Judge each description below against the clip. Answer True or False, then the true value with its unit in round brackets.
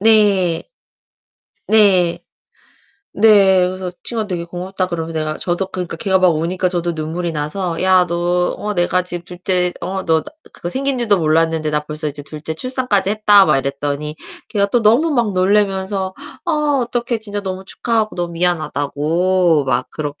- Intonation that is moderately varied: True (3.6 semitones)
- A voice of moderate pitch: True (180 Hz)